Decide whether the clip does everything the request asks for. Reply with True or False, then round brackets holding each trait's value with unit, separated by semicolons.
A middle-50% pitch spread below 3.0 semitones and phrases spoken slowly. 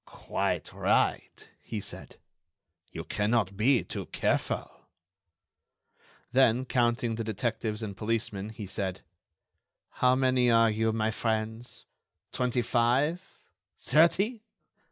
True (2.5 semitones; 105 wpm)